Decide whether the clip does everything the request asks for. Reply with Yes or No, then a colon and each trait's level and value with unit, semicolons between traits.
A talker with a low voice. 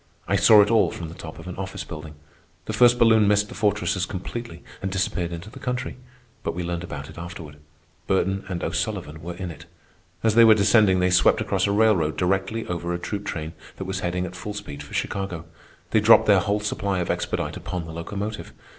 Yes: very low, 95 Hz